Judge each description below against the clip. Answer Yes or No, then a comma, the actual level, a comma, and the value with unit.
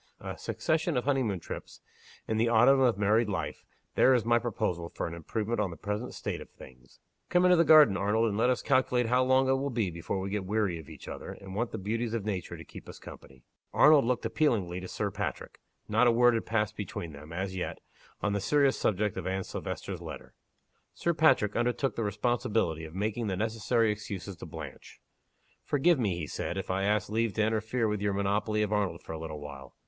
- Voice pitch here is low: Yes, low, 105 Hz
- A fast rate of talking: Yes, fast, 220 wpm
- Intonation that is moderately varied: Yes, average, 4.2 semitones